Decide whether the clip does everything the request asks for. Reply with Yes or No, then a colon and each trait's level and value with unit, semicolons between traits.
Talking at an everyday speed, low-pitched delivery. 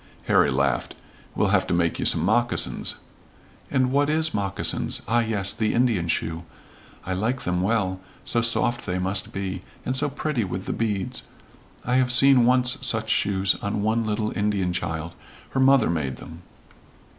Yes: average, 170 wpm; low, 105 Hz